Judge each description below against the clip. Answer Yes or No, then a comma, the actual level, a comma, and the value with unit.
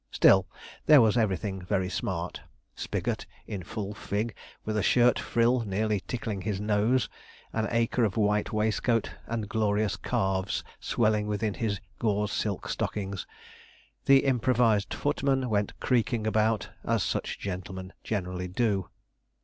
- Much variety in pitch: No, narrow, 2.6 semitones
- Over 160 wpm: No, slow, 135 wpm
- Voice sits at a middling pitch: No, low, 105 Hz